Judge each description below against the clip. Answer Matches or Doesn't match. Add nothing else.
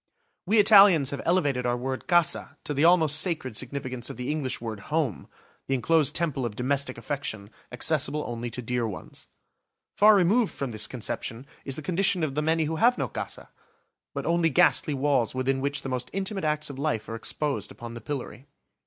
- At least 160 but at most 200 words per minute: Matches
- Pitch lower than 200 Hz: Matches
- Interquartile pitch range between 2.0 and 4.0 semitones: Doesn't match